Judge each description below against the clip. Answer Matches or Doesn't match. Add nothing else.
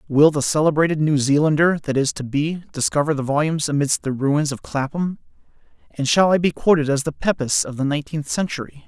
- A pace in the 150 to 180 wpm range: Doesn't match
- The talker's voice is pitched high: Doesn't match